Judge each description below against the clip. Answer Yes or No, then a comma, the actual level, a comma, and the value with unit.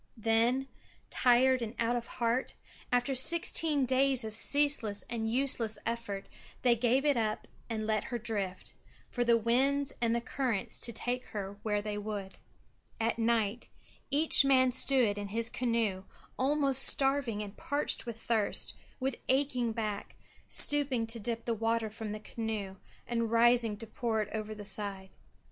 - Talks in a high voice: Yes, high, 230 Hz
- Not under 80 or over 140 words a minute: No, average, 155 wpm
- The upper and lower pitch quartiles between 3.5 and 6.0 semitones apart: No, average, 3.1 semitones